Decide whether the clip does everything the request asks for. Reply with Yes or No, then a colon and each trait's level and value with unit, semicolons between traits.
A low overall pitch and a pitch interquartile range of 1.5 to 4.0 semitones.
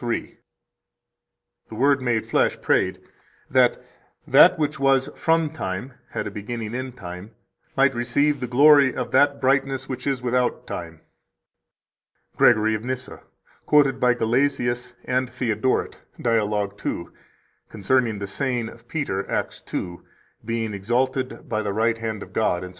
Yes: low, 120 Hz; average, 3.4 semitones